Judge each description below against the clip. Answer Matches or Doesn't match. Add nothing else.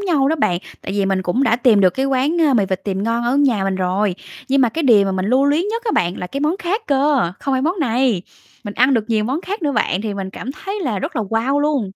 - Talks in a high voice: Matches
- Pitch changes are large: Matches